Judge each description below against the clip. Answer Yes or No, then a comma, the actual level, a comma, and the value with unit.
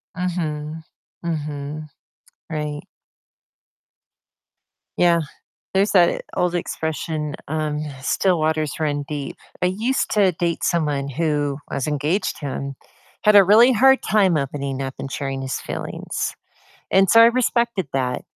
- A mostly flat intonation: No, average, 4.3 semitones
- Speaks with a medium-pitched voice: Yes, medium, 155 Hz